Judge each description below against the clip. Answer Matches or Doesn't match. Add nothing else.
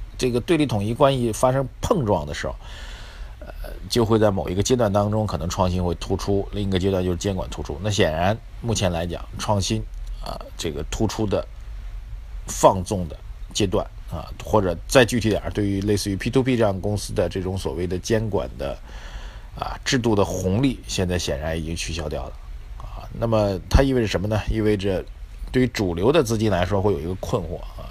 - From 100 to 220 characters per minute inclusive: Doesn't match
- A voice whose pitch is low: Matches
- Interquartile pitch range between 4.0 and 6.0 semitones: Doesn't match